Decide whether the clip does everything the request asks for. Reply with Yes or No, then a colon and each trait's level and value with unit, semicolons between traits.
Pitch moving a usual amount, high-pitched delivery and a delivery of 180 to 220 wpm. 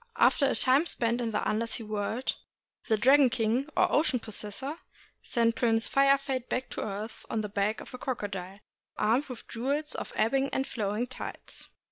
Yes: average, 3.8 semitones; high, 235 Hz; average, 195 wpm